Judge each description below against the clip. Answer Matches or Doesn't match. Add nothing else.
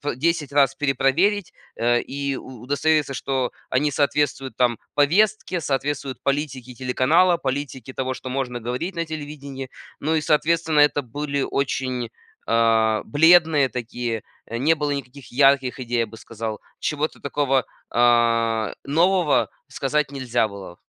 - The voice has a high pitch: Doesn't match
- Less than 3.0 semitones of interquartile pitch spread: Doesn't match